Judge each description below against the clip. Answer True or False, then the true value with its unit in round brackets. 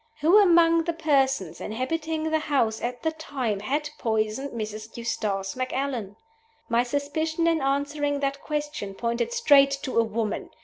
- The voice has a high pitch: True (275 Hz)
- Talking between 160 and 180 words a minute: False (145 wpm)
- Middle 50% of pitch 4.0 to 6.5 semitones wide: True (5.4 semitones)